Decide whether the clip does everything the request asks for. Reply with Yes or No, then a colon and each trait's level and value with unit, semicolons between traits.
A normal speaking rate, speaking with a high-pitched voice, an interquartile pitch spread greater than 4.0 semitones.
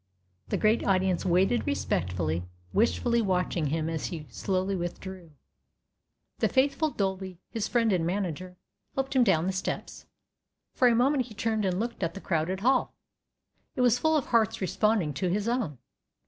Yes: average, 160 wpm; high, 195 Hz; average, 5.1 semitones